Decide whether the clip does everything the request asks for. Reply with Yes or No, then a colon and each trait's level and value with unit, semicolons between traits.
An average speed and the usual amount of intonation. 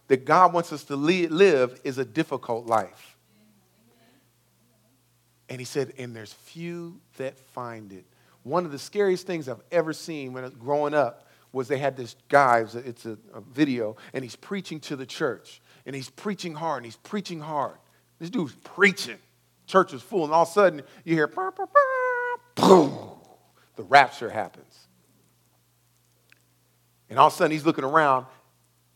No: average, 175 wpm; wide, 6.2 semitones